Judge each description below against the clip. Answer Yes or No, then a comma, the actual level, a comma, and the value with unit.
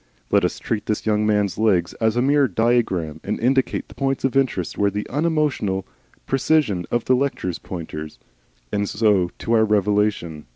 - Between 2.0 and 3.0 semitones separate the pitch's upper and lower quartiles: No, average, 5.0 semitones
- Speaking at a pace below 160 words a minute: No, average, 170 wpm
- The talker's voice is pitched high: No, low, 105 Hz